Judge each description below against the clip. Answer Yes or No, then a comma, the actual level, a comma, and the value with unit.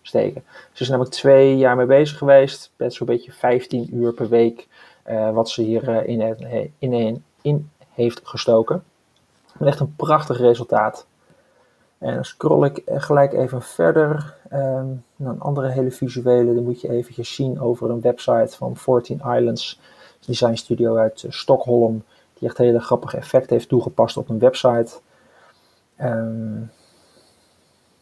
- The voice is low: Yes, low, 125 Hz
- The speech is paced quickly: No, average, 160 wpm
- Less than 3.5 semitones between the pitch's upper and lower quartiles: Yes, narrow, 2.4 semitones